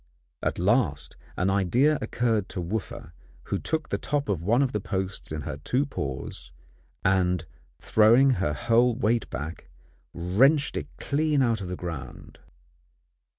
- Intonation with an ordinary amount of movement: No, wide, 6.3 semitones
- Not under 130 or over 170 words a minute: Yes, average, 150 wpm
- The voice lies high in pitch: No, low, 105 Hz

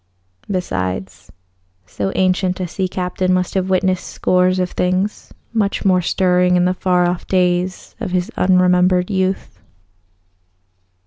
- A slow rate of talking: Yes, slow, 130 wpm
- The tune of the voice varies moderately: No, narrow, 0.7 semitones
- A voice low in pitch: No, medium, 180 Hz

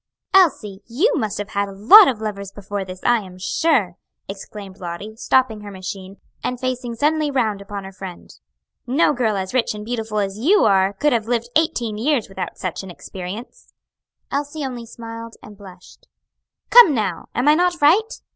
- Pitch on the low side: No, high, 220 Hz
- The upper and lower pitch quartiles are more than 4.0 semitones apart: Yes, average, 4.8 semitones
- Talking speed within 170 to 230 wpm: Yes, average, 175 wpm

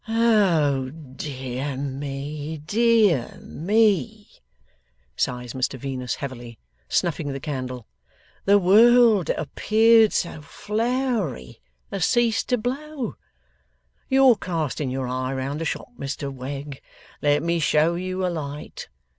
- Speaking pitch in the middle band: Yes, medium, 155 Hz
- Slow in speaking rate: Yes, slow, 115 wpm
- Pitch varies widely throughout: Yes, wide, 8.0 semitones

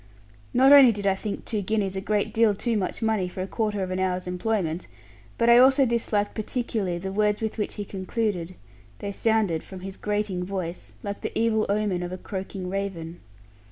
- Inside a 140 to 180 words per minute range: No, average, 195 wpm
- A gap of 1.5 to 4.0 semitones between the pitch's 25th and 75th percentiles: Yes, average, 2.9 semitones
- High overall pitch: Yes, high, 200 Hz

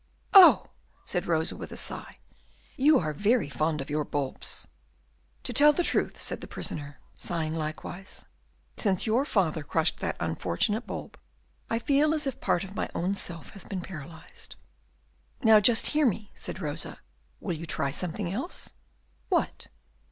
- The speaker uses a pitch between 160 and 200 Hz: Yes, high, 190 Hz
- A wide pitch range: Yes, wide, 6.7 semitones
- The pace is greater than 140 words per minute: Yes, average, 160 wpm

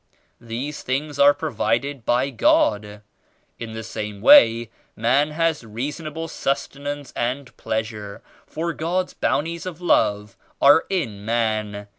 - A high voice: No, low, 130 Hz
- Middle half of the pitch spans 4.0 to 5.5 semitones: Yes, average, 5.2 semitones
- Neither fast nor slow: No, slow, 125 wpm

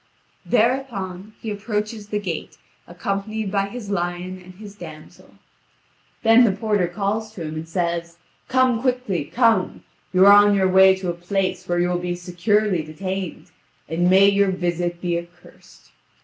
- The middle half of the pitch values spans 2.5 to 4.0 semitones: Yes, average, 3.0 semitones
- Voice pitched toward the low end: No, high, 190 Hz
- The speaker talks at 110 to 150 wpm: No, average, 160 wpm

